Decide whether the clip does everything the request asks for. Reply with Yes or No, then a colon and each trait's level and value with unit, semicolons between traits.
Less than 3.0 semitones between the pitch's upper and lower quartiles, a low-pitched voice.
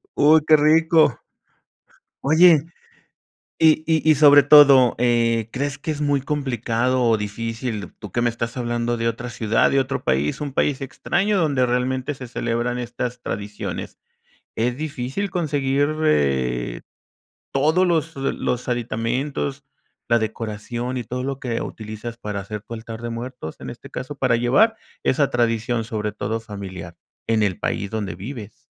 No: average, 4.0 semitones; low, 120 Hz